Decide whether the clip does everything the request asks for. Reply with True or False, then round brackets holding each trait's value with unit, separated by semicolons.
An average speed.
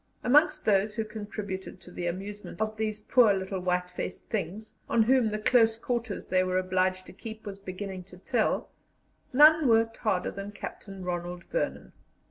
True (170 wpm)